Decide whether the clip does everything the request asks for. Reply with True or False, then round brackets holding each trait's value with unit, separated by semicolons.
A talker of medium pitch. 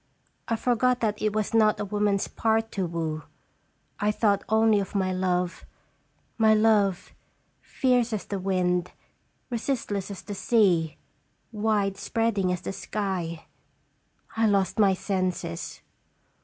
False (205 Hz)